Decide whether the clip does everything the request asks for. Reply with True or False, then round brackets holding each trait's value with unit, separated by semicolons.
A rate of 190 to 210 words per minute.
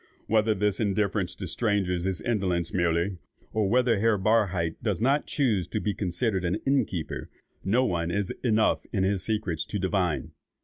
False (170 wpm)